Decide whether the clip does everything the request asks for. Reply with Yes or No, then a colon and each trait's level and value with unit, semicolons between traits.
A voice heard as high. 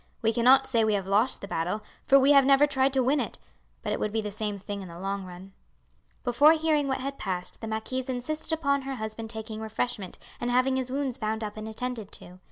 Yes: high, 235 Hz